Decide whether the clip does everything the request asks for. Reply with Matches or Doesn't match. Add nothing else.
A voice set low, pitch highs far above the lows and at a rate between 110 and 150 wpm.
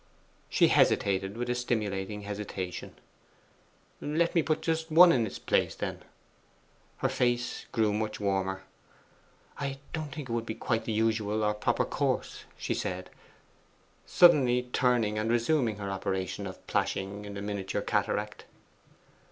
Doesn't match